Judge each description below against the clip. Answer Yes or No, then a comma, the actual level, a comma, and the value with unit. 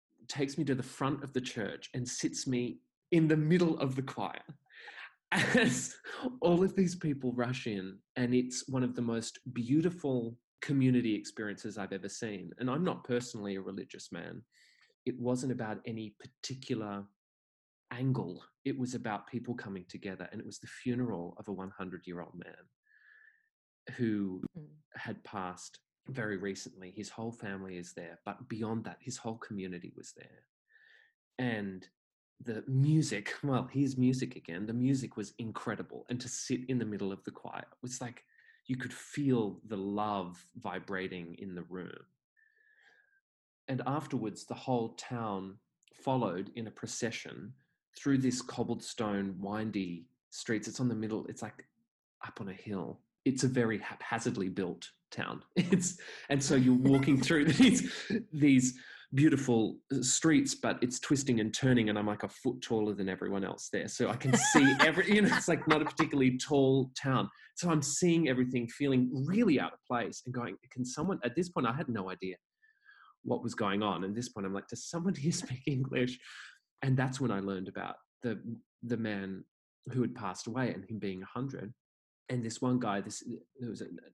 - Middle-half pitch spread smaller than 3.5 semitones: No, average, 5.0 semitones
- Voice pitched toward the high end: No, low, 125 Hz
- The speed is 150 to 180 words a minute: Yes, average, 175 wpm